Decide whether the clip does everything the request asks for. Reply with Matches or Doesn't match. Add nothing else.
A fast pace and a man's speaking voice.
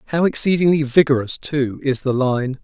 Doesn't match